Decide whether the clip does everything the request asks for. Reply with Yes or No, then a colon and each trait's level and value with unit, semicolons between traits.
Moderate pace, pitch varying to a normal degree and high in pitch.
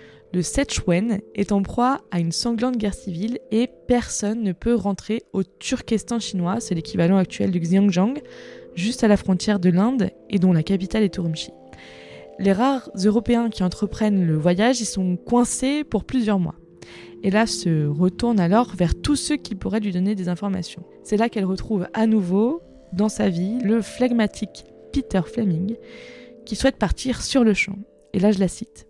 Yes: average, 180 wpm; average, 4.1 semitones; high, 210 Hz